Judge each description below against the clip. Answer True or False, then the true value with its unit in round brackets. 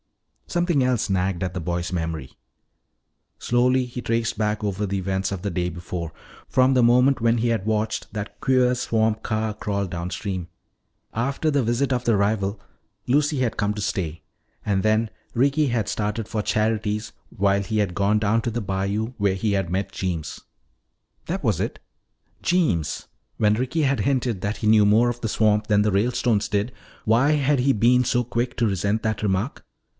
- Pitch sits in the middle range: False (110 Hz)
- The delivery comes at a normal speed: True (180 wpm)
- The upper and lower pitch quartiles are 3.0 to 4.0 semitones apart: True (3.7 semitones)